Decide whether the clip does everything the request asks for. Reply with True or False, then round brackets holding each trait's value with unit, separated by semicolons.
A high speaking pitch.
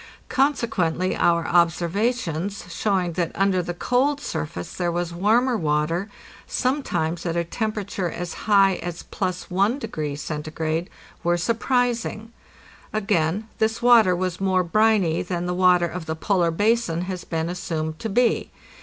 False (180 Hz)